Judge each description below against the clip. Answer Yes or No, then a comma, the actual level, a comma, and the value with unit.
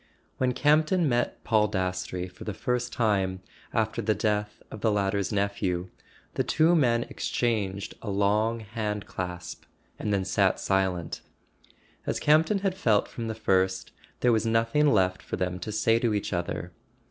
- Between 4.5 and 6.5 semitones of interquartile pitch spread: No, average, 3.5 semitones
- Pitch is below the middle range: Yes, low, 105 Hz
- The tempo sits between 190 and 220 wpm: No, average, 160 wpm